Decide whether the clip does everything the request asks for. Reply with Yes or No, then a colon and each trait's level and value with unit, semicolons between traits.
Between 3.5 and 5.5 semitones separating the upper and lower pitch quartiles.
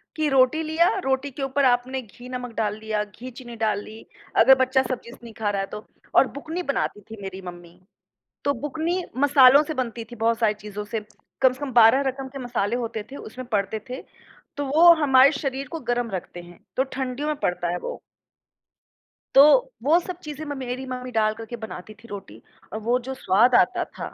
Yes: average, 4.0 semitones